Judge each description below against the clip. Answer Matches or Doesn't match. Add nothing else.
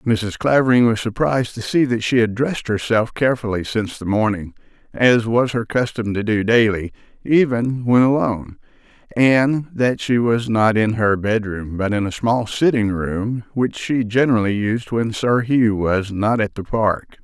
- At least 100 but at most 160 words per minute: Doesn't match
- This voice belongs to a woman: Doesn't match